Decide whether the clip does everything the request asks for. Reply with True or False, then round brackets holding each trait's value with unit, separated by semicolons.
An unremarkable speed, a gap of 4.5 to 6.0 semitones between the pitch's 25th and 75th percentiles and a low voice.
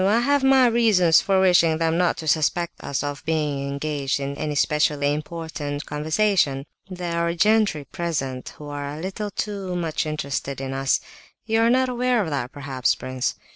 False (175 wpm; 5.3 semitones; 160 Hz)